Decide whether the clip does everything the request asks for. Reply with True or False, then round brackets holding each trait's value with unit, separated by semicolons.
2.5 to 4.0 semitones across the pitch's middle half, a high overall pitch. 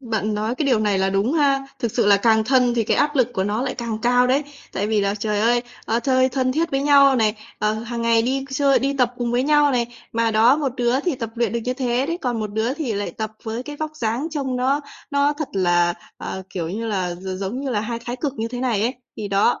True (3.7 semitones; 240 Hz)